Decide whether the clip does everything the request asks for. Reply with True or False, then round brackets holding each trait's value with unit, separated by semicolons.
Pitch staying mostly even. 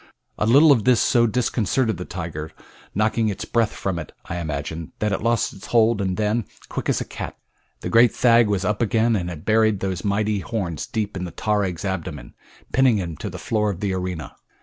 False (3.7 semitones)